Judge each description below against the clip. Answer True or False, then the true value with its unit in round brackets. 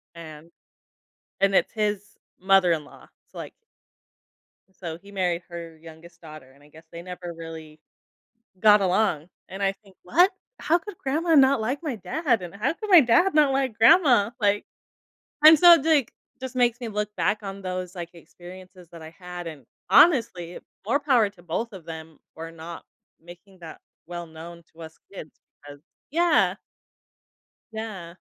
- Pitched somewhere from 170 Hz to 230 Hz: True (190 Hz)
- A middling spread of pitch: False (5.8 semitones)